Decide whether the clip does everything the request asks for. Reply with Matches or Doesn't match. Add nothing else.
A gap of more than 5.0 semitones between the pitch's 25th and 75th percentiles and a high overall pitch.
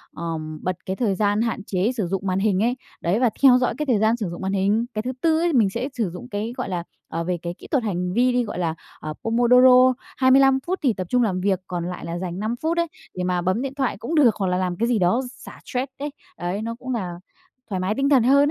Matches